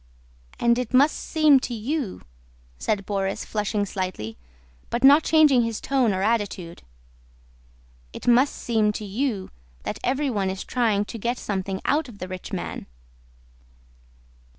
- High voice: Yes, high, 225 Hz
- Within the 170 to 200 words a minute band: No, average, 140 wpm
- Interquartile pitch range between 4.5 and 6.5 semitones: Yes, average, 4.8 semitones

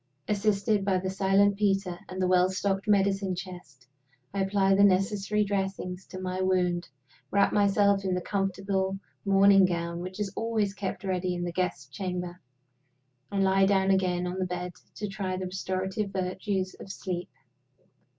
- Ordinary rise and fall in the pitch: No, narrow, 1.4 semitones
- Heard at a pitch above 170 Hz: Yes, high, 190 Hz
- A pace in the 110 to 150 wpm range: No, average, 160 wpm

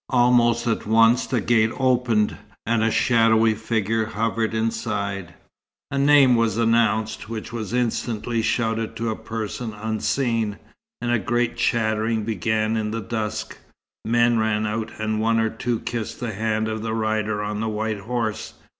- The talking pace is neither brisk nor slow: Yes, average, 155 wpm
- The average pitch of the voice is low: Yes, low, 110 Hz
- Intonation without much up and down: Yes, narrow, 1.3 semitones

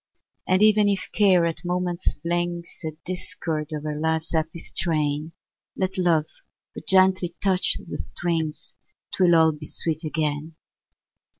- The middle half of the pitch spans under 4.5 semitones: Yes, average, 2.7 semitones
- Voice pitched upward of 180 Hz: No, medium, 170 Hz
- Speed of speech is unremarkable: No, slow, 130 wpm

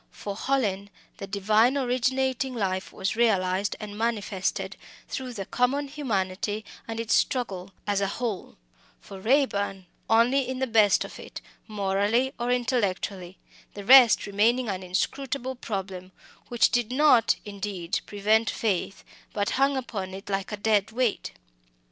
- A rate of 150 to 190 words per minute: No, average, 140 wpm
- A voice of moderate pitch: No, high, 215 Hz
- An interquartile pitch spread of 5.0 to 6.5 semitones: No, average, 4.1 semitones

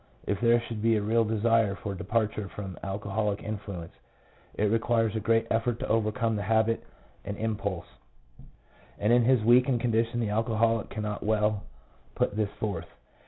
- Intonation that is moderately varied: No, narrow, 1.8 semitones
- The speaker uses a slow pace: No, average, 160 wpm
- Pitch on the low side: Yes, low, 110 Hz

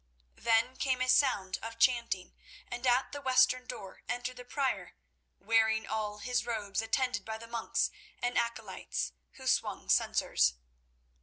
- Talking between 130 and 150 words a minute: Yes, average, 145 wpm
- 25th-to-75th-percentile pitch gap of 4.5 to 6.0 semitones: No, average, 2.8 semitones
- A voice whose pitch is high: Yes, high, 230 Hz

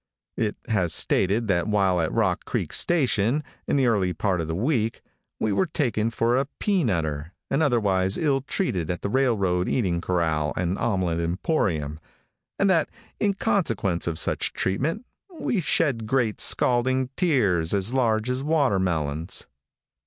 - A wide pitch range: Yes, wide, 6.9 semitones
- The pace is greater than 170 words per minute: No, average, 150 wpm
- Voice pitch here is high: No, low, 105 Hz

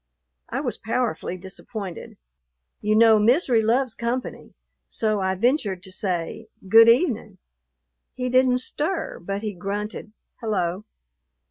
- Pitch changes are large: No, average, 4.0 semitones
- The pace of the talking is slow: Yes, slow, 120 wpm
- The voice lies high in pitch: Yes, high, 220 Hz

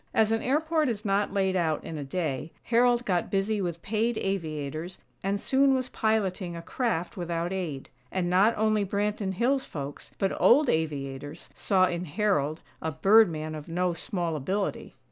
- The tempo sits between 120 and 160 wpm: No, average, 170 wpm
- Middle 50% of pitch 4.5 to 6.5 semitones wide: Yes, average, 5.1 semitones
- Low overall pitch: No, high, 190 Hz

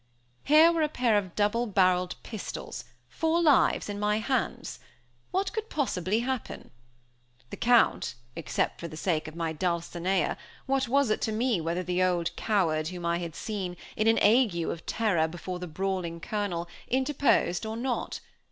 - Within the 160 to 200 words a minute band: Yes, average, 165 wpm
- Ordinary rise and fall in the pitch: No, wide, 5.9 semitones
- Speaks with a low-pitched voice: No, high, 205 Hz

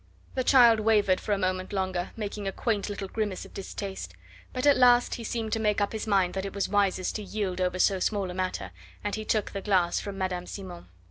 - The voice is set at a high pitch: Yes, high, 200 Hz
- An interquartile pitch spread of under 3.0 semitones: Yes, narrow, 2.5 semitones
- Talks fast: Yes, fast, 230 wpm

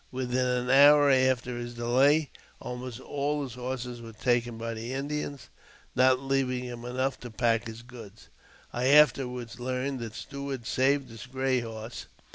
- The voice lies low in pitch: Yes, low, 125 Hz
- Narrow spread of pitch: Yes, narrow, 2.0 semitones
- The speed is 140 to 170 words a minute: Yes, average, 155 wpm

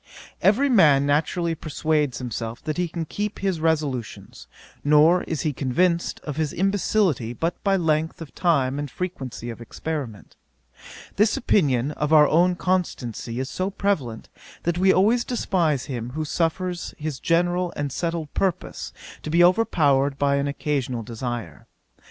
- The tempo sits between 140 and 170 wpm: Yes, average, 150 wpm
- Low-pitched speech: No, medium, 155 Hz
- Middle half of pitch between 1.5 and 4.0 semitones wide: No, average, 4.6 semitones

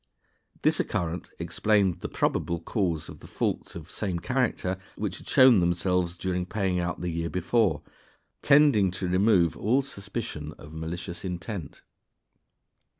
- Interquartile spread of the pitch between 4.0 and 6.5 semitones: No, average, 3.1 semitones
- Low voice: Yes, very low, 90 Hz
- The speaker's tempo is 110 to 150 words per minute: Yes, average, 140 wpm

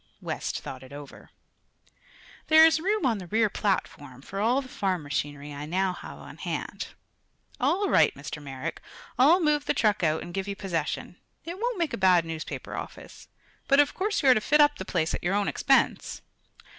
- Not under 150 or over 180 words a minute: No, average, 195 wpm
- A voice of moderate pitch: No, high, 195 Hz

